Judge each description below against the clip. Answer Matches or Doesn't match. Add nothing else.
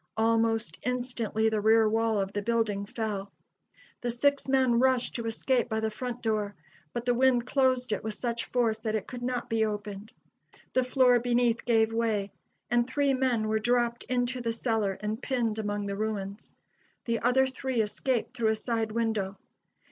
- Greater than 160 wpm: Matches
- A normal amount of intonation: Doesn't match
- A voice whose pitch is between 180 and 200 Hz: Doesn't match